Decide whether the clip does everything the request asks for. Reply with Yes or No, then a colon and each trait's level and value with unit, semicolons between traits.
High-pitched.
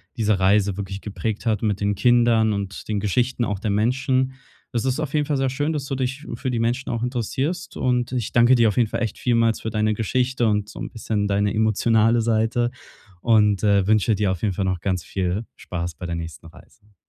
No: low, 110 Hz